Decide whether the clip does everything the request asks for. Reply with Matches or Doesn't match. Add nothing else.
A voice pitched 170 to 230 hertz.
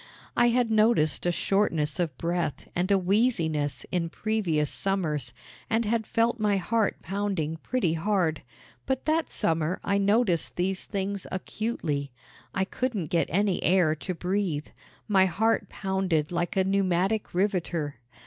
Matches